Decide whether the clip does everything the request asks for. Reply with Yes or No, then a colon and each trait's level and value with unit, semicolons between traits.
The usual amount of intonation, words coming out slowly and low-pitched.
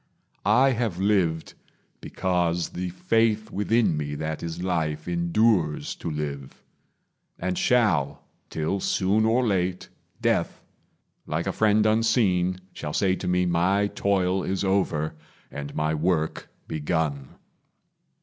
Yes: average, 4.4 semitones; slow, 120 wpm; very low, 90 Hz